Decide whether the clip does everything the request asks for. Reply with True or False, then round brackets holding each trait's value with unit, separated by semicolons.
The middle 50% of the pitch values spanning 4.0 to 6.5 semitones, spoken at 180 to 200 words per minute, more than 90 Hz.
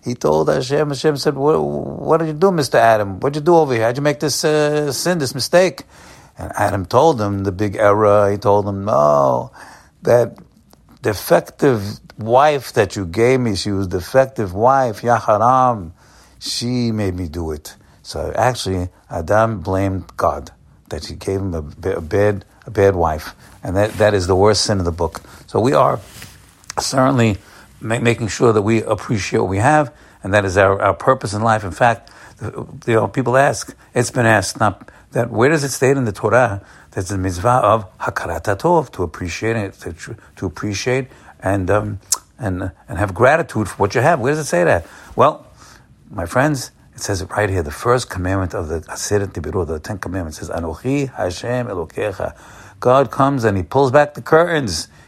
True (5.1 semitones; 190 wpm; 105 Hz)